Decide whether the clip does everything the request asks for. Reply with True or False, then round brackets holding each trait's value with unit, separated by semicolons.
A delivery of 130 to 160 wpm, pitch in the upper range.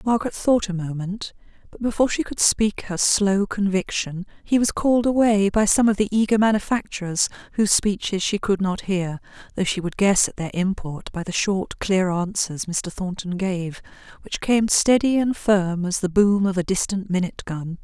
False (185 wpm; 195 Hz)